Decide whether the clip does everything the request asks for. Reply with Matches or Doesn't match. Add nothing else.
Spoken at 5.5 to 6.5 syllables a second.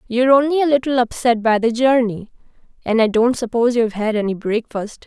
Matches